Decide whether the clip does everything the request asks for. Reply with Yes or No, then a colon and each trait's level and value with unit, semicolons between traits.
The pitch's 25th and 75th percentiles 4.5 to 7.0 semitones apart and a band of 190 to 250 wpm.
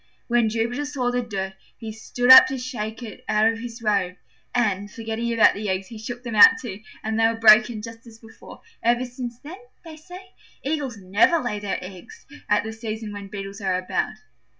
No: average, 2.8 semitones; average, 200 wpm